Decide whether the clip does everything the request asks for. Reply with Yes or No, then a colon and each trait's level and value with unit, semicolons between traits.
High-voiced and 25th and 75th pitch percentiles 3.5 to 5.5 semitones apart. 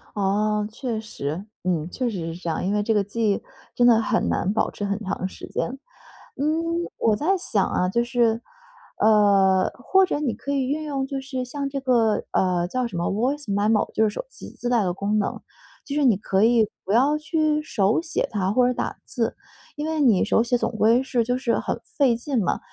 Yes: high, 225 Hz; average, 5.0 semitones